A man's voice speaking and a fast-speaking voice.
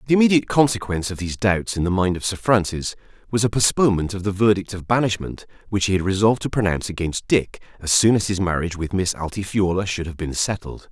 Yes: male; fast, 220 wpm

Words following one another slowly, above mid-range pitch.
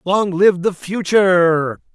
No: slow, 125 wpm; medium, 180 Hz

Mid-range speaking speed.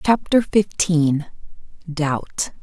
No: slow, 70 wpm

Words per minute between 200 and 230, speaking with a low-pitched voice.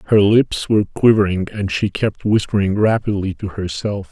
No: average, 160 wpm; low, 100 Hz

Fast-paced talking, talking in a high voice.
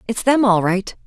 Yes: fast, 225 wpm; high, 215 Hz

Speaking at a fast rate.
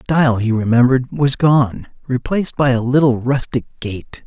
No: average, 170 wpm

